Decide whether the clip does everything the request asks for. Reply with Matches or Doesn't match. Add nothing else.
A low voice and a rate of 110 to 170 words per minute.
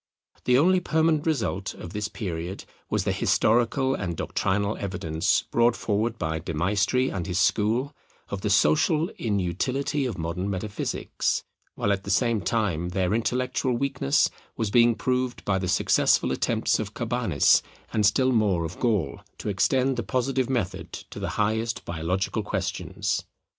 Matches